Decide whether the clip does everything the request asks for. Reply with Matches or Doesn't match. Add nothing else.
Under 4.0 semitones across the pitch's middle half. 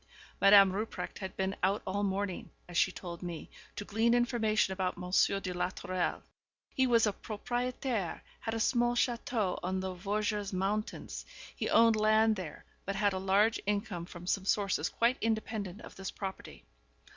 Matches